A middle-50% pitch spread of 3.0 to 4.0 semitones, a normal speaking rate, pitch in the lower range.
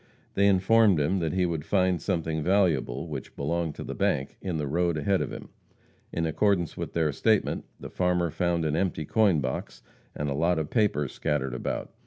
Yes: average, 3.7 semitones; average, 195 wpm; very low, 85 Hz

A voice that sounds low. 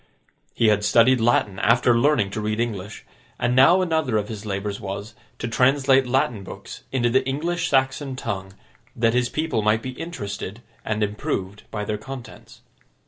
Yes: low, 115 Hz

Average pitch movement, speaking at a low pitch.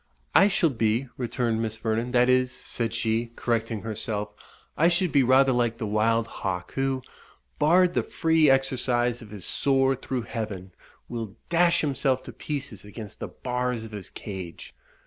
Yes: average, 3.2 semitones; low, 120 Hz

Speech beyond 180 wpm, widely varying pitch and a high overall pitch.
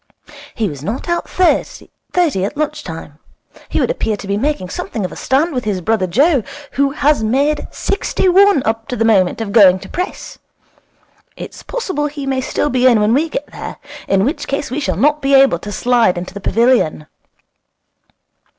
Yes: average, 190 wpm; wide, 6.4 semitones; high, 245 Hz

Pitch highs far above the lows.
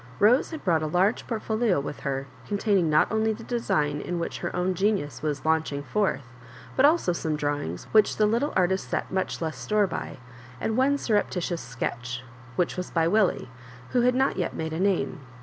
Yes: wide, 6.0 semitones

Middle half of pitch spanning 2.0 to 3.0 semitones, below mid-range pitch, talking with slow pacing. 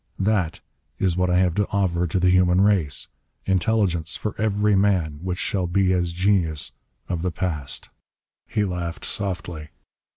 No: narrow, 2.4 semitones; very low, 90 Hz; average, 160 wpm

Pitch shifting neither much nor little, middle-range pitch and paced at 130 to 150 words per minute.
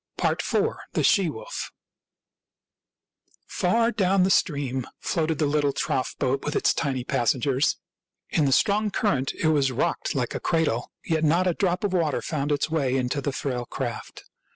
No: average, 4.9 semitones; medium, 150 Hz; average, 170 wpm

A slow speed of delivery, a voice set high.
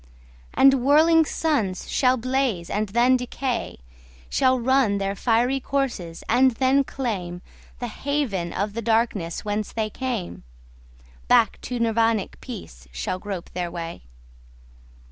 Yes: slow, 115 wpm; high, 220 Hz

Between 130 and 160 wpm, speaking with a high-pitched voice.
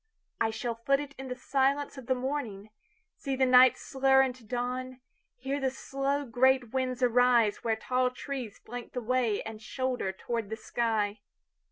Yes: average, 145 wpm; very high, 250 Hz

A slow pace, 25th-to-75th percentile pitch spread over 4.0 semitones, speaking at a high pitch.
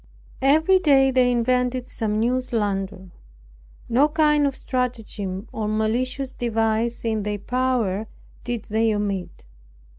No: slow, 120 wpm; average, 3.1 semitones; high, 235 Hz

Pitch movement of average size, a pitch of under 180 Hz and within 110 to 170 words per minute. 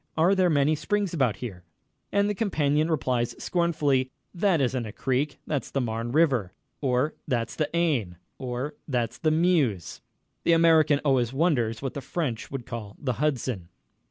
Yes: average, 4.9 semitones; medium, 140 Hz; average, 160 wpm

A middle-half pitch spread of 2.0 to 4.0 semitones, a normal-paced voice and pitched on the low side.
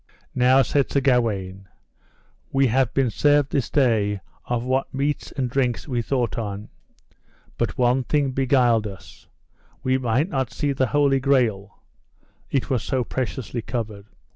Yes: average, 3.0 semitones; average, 145 wpm; low, 125 Hz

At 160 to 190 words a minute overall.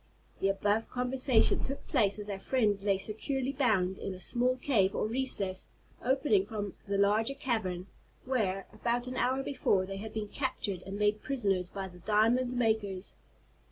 Yes: average, 165 wpm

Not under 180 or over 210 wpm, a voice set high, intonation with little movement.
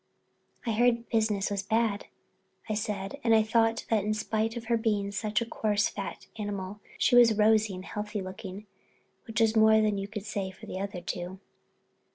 Yes: average, 185 wpm; high, 215 Hz; narrow, 2.0 semitones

